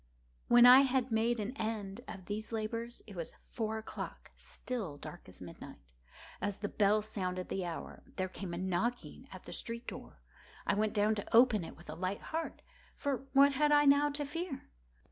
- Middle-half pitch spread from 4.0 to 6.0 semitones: Yes, average, 4.5 semitones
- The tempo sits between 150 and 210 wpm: Yes, average, 185 wpm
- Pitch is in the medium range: No, high, 220 Hz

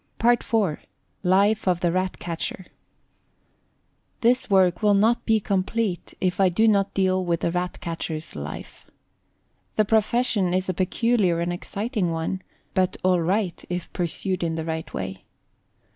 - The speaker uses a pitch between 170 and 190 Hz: Yes, medium, 185 Hz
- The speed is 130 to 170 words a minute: Yes, average, 150 wpm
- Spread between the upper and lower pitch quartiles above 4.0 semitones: No, average, 3.2 semitones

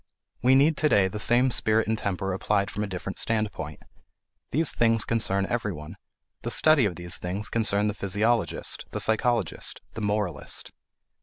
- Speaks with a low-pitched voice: Yes, low, 105 Hz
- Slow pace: No, average, 160 wpm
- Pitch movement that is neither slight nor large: Yes, average, 3.0 semitones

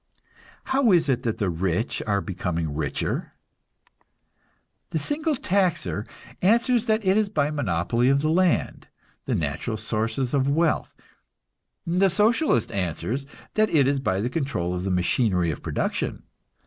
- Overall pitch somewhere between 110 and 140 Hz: Yes, low, 135 Hz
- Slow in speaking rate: No, average, 145 wpm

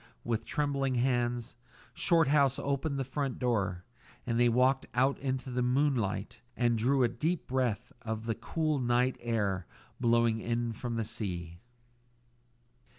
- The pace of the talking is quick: No, average, 140 wpm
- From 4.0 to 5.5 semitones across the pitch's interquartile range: No, average, 2.8 semitones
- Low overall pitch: Yes, low, 120 Hz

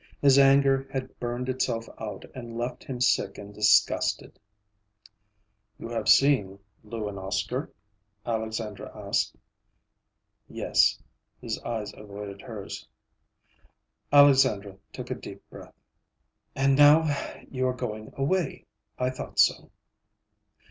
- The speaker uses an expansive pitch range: No, average, 4.2 semitones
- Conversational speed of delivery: No, slow, 115 wpm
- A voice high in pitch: No, low, 120 Hz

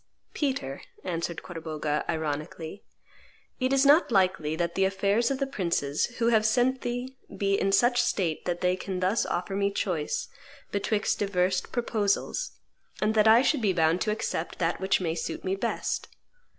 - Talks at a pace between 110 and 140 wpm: No, average, 165 wpm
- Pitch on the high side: Yes, high, 195 Hz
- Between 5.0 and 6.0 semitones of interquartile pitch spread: Yes, average, 5.3 semitones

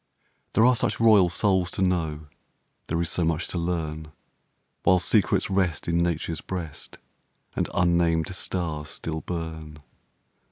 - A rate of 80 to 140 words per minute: Yes, slow, 135 wpm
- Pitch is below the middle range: Yes, very low, 85 Hz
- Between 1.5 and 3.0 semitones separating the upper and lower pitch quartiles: Yes, narrow, 2.5 semitones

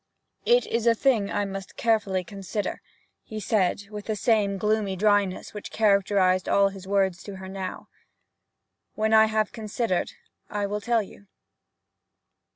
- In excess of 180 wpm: No, average, 150 wpm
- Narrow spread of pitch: Yes, narrow, 2.0 semitones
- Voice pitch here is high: Yes, high, 205 Hz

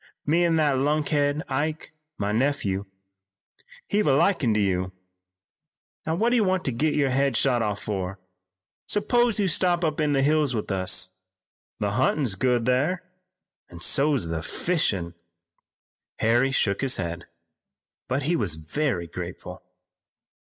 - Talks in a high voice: No, low, 135 Hz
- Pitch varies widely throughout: Yes, wide, 7.3 semitones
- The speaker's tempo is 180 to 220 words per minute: No, average, 150 wpm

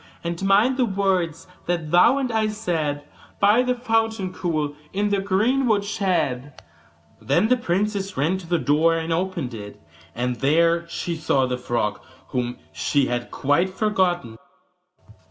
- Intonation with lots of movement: Yes, wide, 5.9 semitones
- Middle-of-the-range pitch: Yes, medium, 175 Hz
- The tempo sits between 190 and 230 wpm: No, average, 150 wpm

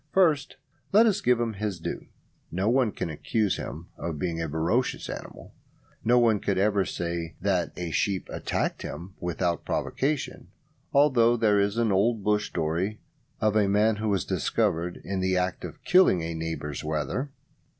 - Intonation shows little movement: No, average, 5.1 semitones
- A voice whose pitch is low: Yes, low, 100 Hz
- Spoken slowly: No, average, 170 wpm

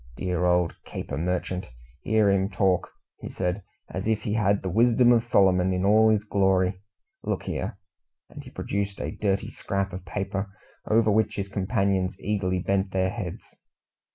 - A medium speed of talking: Yes, average, 165 wpm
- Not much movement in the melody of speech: Yes, narrow, 2.0 semitones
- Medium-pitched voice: No, very low, 95 Hz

